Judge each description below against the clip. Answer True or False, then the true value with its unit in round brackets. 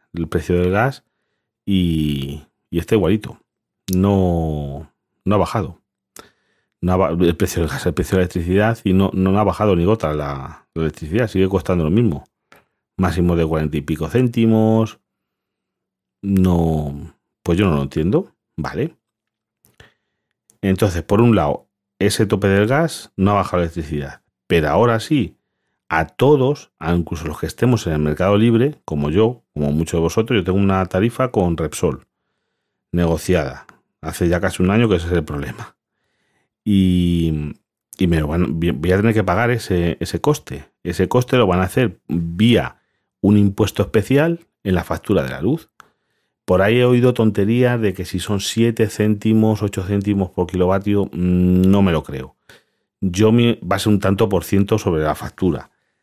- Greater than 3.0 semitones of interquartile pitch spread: True (4.4 semitones)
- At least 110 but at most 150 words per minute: False (170 wpm)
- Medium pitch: False (95 Hz)